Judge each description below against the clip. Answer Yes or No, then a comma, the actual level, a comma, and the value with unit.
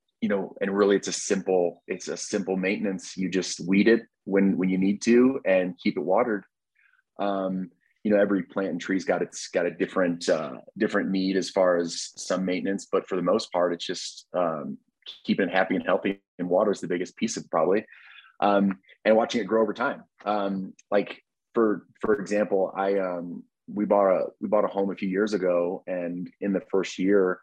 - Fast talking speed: Yes, fast, 210 wpm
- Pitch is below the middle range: Yes, very low, 95 Hz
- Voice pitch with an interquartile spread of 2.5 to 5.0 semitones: No, narrow, 1.7 semitones